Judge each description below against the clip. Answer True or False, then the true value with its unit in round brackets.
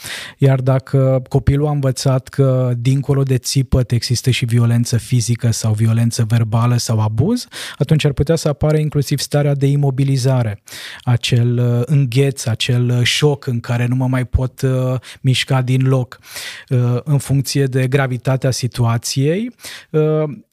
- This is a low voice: True (130 Hz)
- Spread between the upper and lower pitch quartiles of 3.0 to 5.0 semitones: False (2.4 semitones)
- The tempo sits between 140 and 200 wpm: False (130 wpm)